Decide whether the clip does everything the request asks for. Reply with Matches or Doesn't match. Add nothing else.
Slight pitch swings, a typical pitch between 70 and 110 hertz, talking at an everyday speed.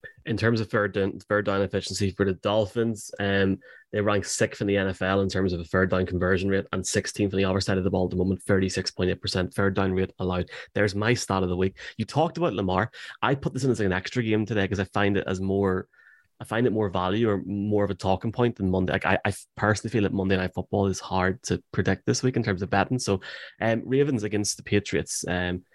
Doesn't match